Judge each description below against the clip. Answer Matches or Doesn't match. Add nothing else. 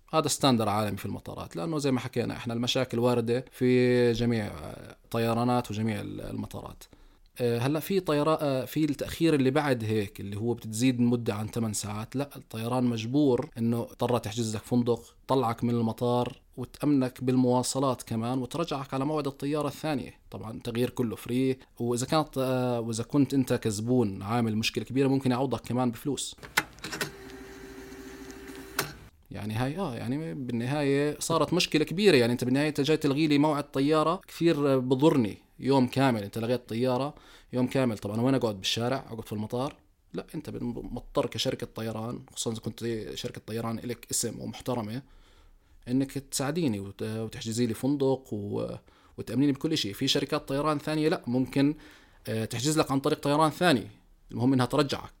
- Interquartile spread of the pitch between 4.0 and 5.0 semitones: Doesn't match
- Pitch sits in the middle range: Doesn't match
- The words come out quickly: Matches